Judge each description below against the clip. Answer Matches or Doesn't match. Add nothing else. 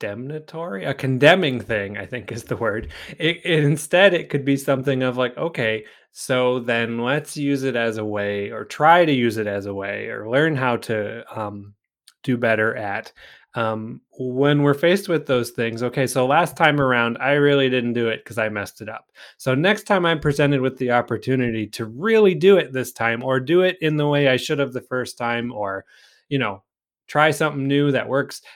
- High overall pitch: Doesn't match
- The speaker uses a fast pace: Matches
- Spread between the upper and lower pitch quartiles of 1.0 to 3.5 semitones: Doesn't match